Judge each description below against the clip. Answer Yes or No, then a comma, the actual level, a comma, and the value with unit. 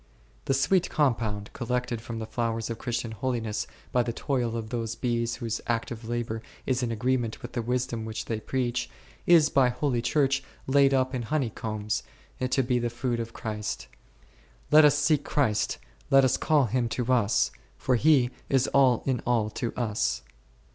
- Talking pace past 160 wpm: Yes, average, 175 wpm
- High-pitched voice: No, low, 120 Hz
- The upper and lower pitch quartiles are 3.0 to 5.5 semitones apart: No, narrow, 2.5 semitones